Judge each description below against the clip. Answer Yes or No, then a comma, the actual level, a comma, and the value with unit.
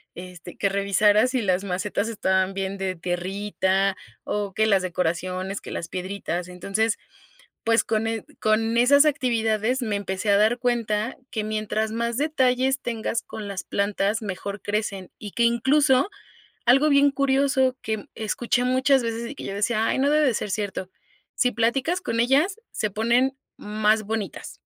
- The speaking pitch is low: No, high, 220 Hz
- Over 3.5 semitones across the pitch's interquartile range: Yes, average, 4.0 semitones